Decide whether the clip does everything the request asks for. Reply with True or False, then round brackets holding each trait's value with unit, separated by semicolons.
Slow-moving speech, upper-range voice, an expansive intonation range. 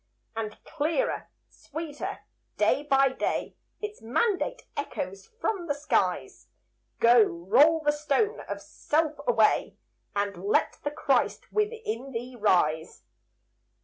True (115 wpm; 285 Hz; 6.9 semitones)